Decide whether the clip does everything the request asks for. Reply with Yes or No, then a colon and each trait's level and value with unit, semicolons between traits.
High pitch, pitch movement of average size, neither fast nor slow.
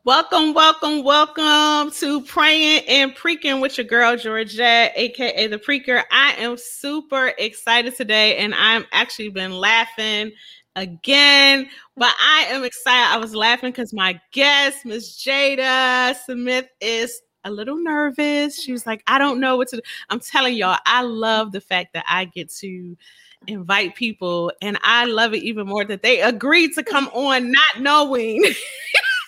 Yes: very high, 250 Hz; average, 4.3 semitones; average, 160 wpm